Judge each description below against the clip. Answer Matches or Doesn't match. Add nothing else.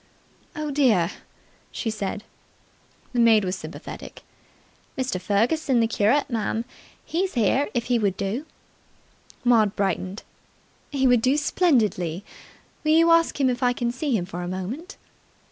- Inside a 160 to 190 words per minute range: Doesn't match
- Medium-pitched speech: Doesn't match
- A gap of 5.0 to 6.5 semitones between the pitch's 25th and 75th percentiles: Matches